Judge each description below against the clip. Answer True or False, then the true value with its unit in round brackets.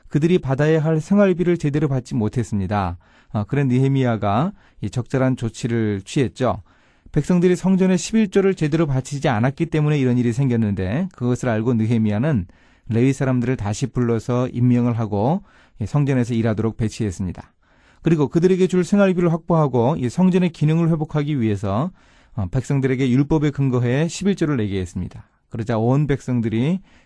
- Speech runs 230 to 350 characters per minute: False (365 characters per minute)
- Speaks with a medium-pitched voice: False (130 Hz)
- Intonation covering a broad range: True (5.8 semitones)